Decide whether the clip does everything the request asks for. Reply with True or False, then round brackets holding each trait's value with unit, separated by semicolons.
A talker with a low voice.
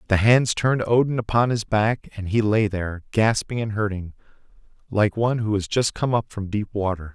True (105 Hz)